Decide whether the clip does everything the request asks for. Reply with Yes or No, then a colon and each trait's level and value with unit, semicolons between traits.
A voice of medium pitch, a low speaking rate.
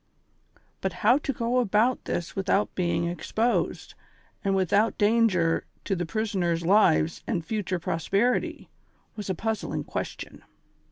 No: high, 200 Hz; slow, 130 wpm